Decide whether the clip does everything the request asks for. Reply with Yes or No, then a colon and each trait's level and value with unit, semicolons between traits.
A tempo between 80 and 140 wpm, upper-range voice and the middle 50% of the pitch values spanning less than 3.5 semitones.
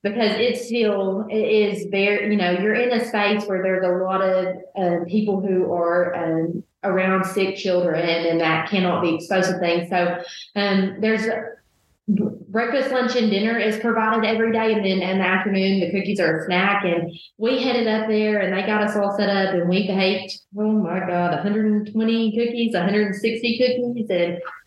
No: average, 190 wpm; high, 200 Hz; average, 3.0 semitones